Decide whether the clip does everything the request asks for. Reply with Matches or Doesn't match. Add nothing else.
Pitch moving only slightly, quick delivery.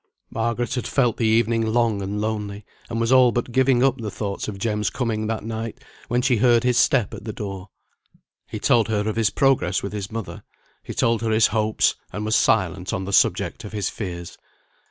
Matches